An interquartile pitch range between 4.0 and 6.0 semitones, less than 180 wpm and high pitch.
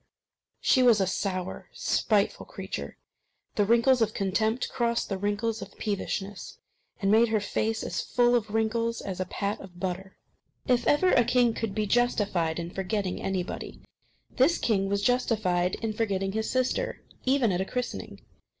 No: average, 3.5 semitones; average, 160 wpm; high, 215 Hz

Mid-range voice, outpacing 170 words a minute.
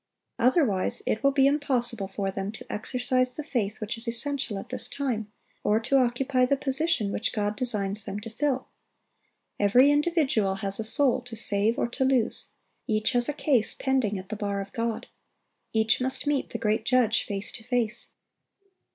No: high, 235 Hz; average, 180 wpm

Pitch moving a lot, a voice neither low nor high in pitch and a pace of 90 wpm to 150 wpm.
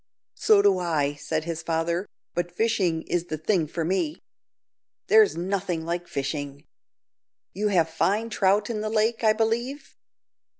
No: average, 4.8 semitones; medium, 180 Hz; average, 145 wpm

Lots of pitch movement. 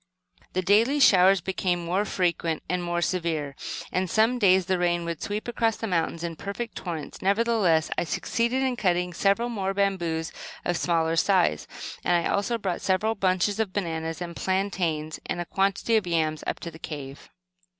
No: average, 3.1 semitones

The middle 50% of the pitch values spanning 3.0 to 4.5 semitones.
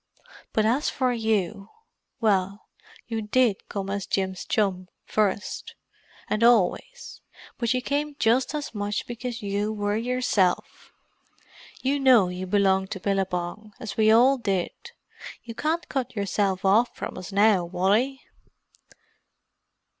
Yes: average, 4.0 semitones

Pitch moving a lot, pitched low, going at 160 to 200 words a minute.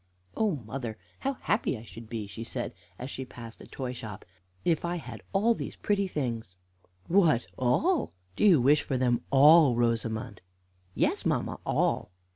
Yes: wide, 6.8 semitones; low, 130 Hz; average, 165 wpm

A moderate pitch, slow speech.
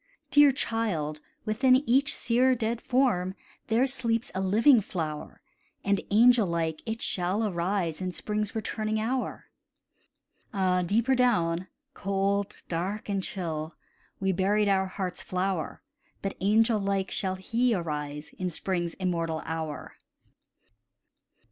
No: high, 195 Hz; slow, 125 wpm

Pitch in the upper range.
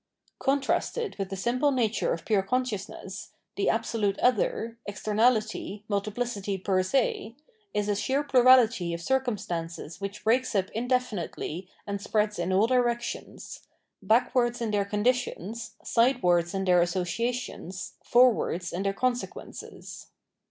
Yes: high, 215 Hz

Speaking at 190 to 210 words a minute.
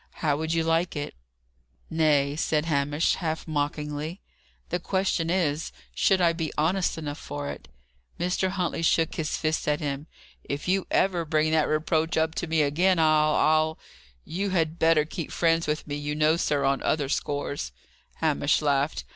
No: average, 170 wpm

